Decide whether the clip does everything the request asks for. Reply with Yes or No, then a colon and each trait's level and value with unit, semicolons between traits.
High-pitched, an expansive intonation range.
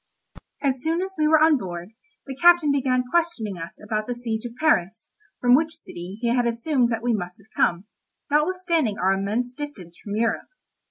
Yes: high, 245 Hz; wide, 6.5 semitones